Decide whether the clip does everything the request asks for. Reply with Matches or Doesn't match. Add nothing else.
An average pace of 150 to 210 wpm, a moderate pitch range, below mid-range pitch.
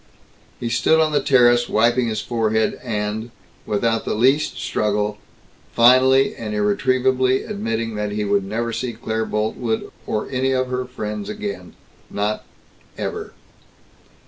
Doesn't match